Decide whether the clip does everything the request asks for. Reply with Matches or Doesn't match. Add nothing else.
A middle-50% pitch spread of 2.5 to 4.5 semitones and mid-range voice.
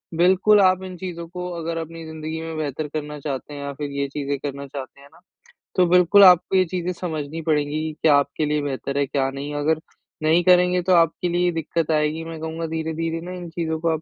Matches